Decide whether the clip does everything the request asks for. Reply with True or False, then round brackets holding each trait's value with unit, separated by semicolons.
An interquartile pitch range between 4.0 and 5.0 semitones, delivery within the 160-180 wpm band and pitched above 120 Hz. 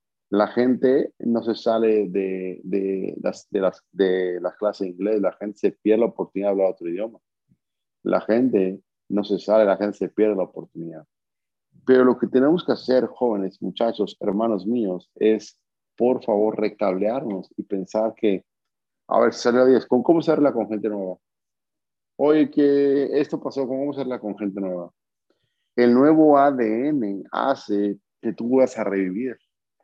False (4.3 semitones; 165 wpm; 110 Hz)